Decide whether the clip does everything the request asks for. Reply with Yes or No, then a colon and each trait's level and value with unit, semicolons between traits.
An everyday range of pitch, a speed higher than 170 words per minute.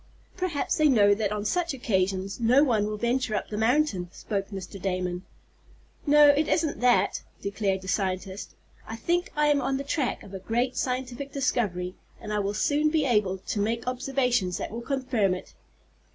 No: wide, 5.7 semitones; average, 180 wpm